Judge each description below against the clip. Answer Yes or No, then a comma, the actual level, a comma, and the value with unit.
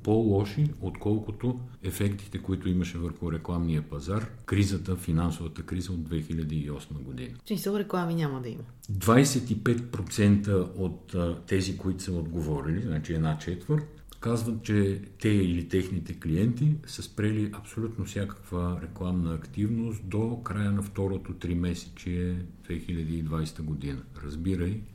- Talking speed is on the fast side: No, average, 120 wpm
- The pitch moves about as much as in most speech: Yes, average, 4.2 semitones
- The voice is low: Yes, very low, 95 Hz